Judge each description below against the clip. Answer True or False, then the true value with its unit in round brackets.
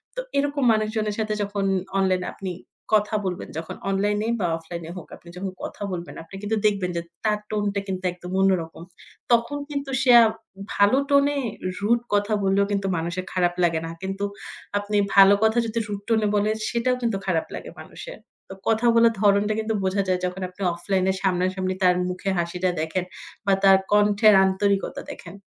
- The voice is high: True (200 Hz)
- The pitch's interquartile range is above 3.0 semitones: False (2.7 semitones)